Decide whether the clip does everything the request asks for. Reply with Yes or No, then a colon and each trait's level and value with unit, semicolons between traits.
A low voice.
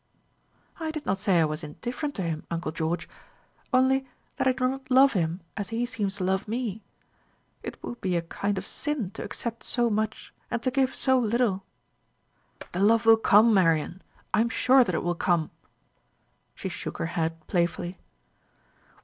No: high, 205 Hz